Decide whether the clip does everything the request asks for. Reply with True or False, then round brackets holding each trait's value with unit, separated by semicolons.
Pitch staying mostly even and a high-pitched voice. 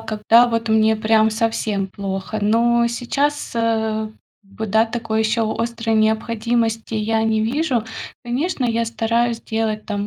True (1.2 semitones; 225 Hz)